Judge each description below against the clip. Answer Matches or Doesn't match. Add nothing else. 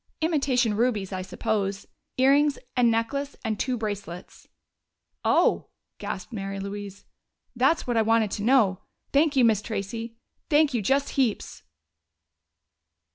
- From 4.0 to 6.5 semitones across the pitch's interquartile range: Matches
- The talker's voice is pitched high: Matches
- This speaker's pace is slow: Matches